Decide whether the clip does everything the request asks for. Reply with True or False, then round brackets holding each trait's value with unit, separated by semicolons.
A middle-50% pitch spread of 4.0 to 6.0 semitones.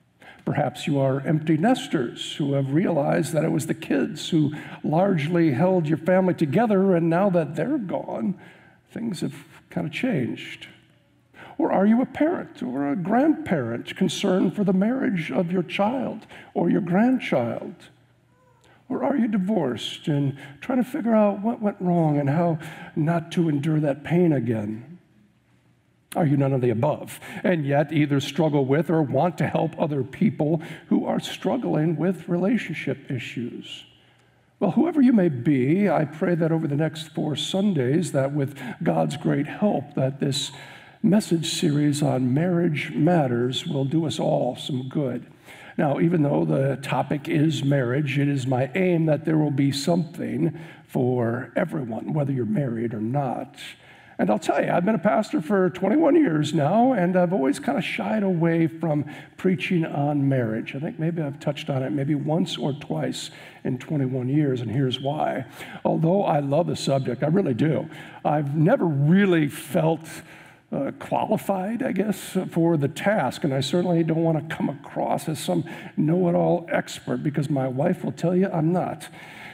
True (4.3 semitones)